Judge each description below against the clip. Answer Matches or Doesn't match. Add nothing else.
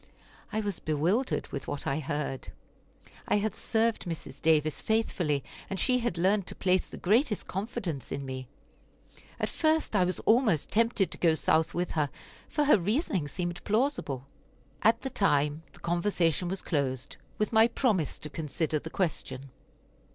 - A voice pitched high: Doesn't match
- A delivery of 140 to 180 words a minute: Matches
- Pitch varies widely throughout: Matches